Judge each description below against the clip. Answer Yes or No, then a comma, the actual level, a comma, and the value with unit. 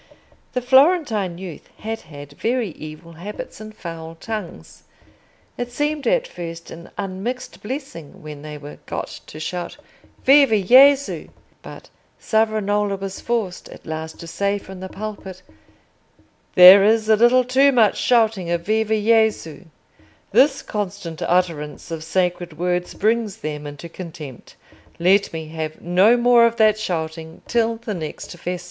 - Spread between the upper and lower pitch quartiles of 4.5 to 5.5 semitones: Yes, average, 5.2 semitones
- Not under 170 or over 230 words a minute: No, average, 145 wpm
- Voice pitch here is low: No, high, 195 Hz